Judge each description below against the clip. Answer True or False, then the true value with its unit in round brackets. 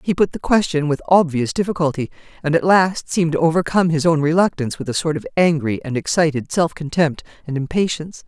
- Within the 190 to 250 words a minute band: True (195 wpm)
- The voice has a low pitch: False (160 Hz)